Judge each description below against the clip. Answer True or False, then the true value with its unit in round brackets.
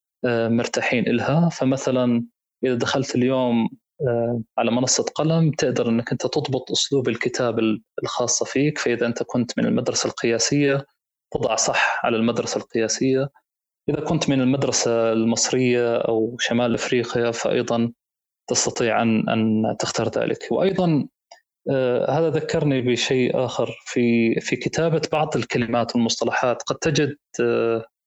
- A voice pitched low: True (125 Hz)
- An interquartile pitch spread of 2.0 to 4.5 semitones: True (2.9 semitones)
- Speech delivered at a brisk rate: False (120 wpm)